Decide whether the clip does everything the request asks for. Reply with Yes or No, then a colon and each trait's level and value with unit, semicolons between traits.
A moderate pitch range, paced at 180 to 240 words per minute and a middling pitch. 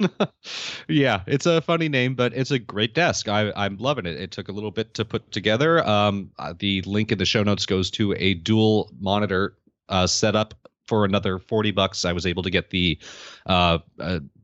No: average, 3.2 semitones; average, 200 wpm; low, 105 Hz